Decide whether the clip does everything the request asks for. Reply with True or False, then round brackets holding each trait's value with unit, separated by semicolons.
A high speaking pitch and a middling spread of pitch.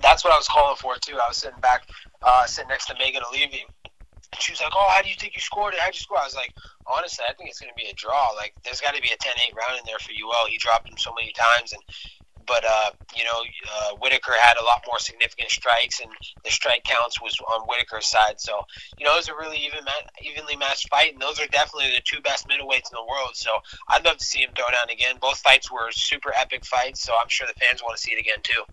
False (120 Hz; 4.7 semitones)